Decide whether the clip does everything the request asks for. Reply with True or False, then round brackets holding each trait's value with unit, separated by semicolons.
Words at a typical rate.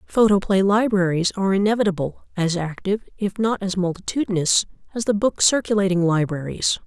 False (130 wpm)